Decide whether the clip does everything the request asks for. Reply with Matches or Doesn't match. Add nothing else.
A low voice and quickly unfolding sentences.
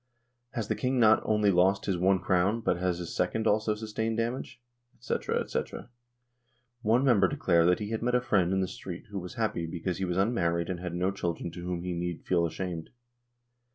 Matches